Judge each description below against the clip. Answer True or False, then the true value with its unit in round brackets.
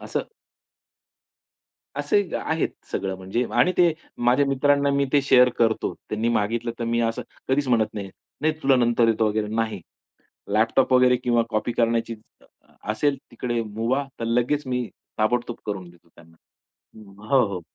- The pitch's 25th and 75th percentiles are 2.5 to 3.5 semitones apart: True (3.0 semitones)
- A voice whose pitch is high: False (115 Hz)